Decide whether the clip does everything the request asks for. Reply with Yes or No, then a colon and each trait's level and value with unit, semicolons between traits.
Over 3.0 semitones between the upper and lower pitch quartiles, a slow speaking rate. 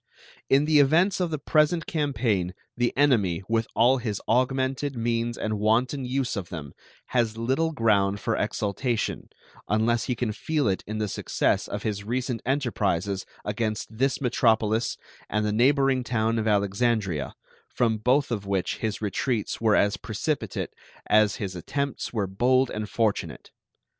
No: average, 3.9 semitones; average, 155 wpm